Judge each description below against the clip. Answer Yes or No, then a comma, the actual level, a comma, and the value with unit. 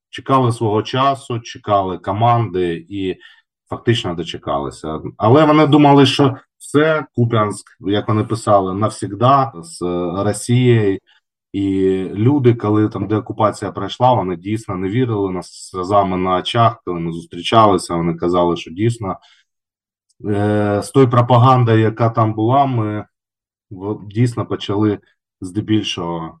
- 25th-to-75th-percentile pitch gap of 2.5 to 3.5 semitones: No, average, 4.1 semitones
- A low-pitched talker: Yes, low, 105 Hz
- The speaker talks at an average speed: Yes, average, 120 wpm